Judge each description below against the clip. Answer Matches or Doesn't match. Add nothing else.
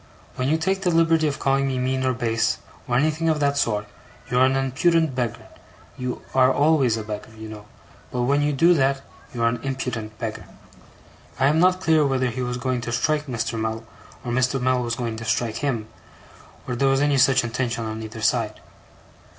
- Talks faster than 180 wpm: Matches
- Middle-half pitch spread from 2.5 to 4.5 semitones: Matches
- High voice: Doesn't match